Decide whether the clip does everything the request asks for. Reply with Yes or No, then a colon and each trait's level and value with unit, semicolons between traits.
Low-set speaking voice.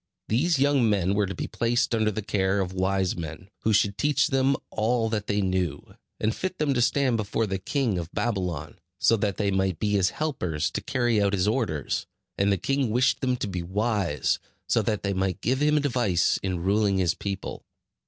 Yes: low, 105 Hz